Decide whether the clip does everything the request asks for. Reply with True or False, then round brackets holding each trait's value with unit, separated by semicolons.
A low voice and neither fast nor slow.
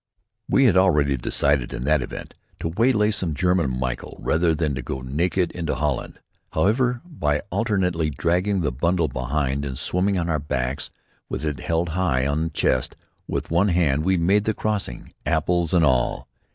True (80 Hz; 175 wpm)